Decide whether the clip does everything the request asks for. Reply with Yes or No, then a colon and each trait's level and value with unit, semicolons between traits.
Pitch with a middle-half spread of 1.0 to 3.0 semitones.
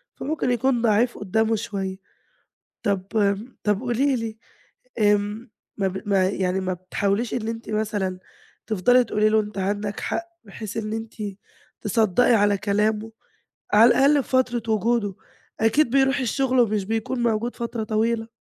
Yes: average, 2.7 semitones